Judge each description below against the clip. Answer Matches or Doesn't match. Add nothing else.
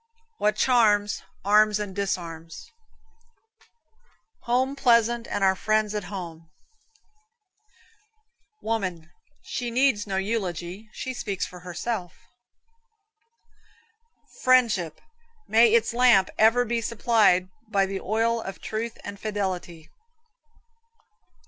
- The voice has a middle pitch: Doesn't match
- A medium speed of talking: Doesn't match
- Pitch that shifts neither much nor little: Matches